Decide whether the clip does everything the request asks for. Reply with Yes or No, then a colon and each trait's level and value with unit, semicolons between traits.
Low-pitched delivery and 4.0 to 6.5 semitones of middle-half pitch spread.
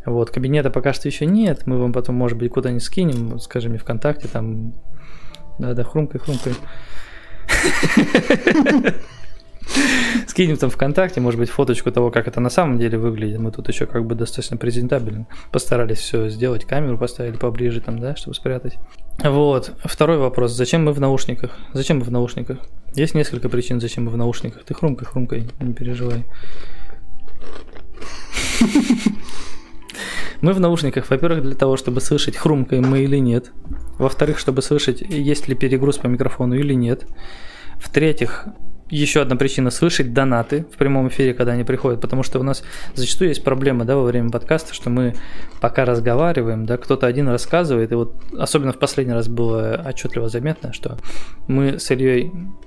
No: low, 130 Hz; average, 3.0 semitones